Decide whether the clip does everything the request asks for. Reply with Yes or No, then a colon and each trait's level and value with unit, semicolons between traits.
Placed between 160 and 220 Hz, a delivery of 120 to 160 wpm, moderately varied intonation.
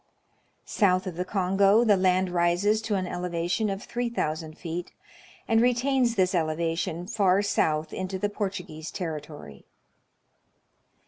Yes: medium, 185 Hz; slow, 135 wpm; average, 3.5 semitones